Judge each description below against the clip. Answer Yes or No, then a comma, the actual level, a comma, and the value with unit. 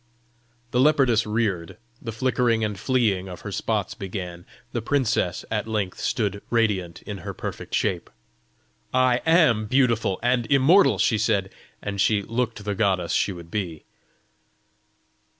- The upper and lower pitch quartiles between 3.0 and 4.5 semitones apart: Yes, average, 4.1 semitones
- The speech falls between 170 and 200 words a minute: No, average, 140 wpm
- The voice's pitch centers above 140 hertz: No, low, 110 Hz